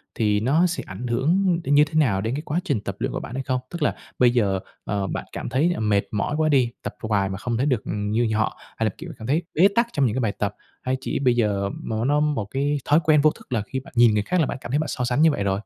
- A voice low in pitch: Yes, low, 125 Hz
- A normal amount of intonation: No, wide, 5.7 semitones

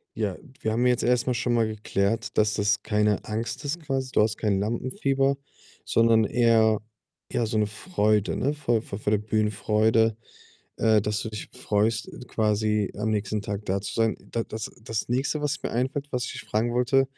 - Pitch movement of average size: No, narrow, 2.3 semitones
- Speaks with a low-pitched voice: Yes, low, 110 Hz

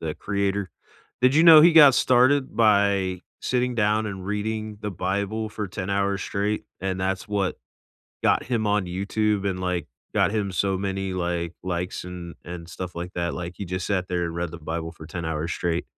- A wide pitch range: No, average, 3.0 semitones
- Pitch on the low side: Yes, very low, 95 Hz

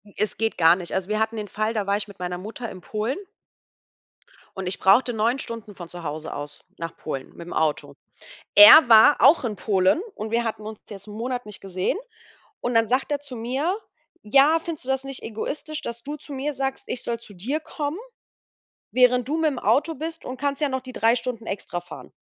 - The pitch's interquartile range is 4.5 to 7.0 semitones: Yes, average, 5.1 semitones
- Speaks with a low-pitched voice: No, high, 230 Hz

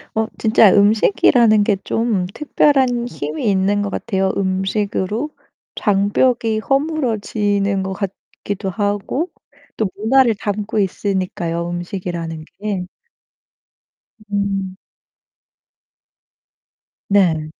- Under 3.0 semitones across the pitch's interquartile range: Yes, narrow, 2.6 semitones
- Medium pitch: No, high, 205 Hz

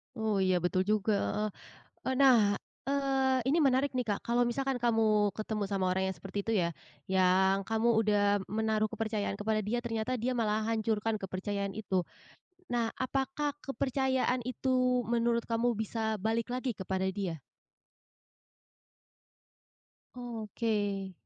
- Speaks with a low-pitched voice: No, high, 220 Hz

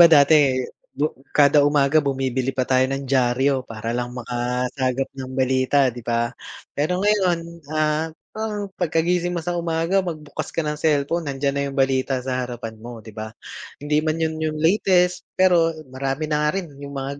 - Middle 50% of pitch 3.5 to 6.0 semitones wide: Yes, average, 4.0 semitones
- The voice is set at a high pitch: No, medium, 145 Hz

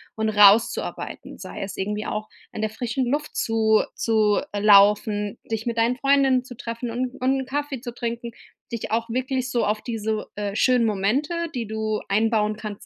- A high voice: Yes, high, 225 Hz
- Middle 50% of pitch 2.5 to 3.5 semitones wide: Yes, average, 2.8 semitones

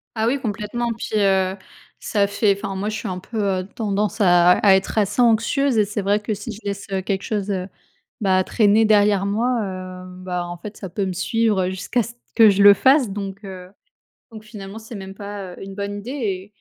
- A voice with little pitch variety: Yes, narrow, 2.2 semitones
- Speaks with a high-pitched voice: Yes, high, 200 Hz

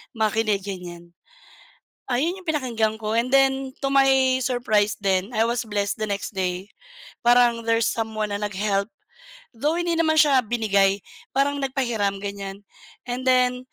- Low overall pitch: No, high, 225 Hz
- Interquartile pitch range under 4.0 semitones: No, average, 4.4 semitones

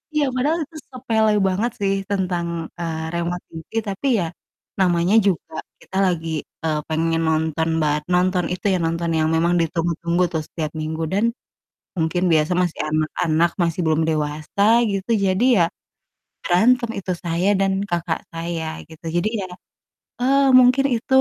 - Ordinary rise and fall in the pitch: Yes, average, 3.3 semitones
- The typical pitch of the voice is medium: Yes, medium, 175 Hz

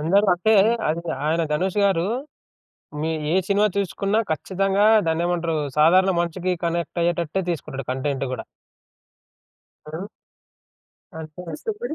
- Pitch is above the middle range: No, medium, 170 Hz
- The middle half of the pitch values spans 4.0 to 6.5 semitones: No, average, 3.5 semitones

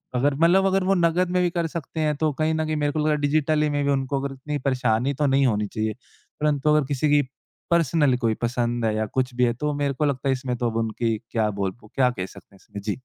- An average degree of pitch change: Yes, average, 4.1 semitones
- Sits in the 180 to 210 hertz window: No, medium, 140 Hz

